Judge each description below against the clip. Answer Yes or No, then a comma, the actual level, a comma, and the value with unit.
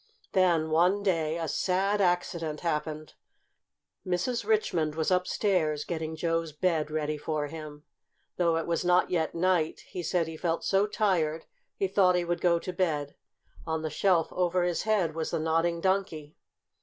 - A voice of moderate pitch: Yes, medium, 170 Hz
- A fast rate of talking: No, average, 165 wpm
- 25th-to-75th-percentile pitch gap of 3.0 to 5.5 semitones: No, narrow, 2.6 semitones